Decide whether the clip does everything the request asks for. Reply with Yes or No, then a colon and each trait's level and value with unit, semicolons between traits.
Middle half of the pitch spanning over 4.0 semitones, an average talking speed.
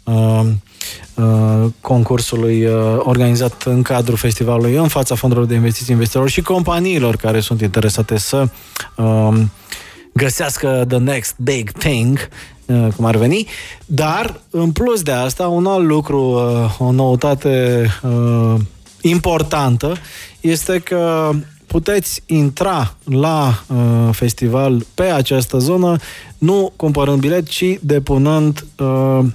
No: average, 4.8 semitones; slow, 100 wpm